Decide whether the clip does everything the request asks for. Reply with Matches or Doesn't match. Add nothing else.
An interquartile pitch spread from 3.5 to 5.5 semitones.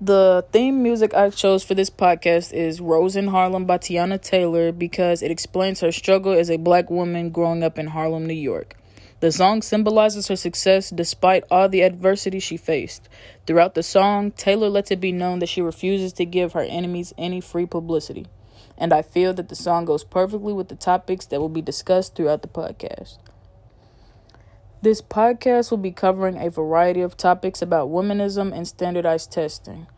Doesn't match